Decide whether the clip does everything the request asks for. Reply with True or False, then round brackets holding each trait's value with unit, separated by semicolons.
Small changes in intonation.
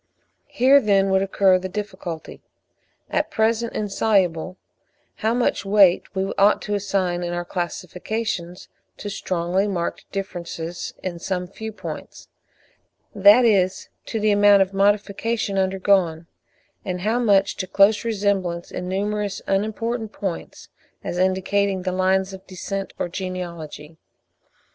True (2.2 semitones)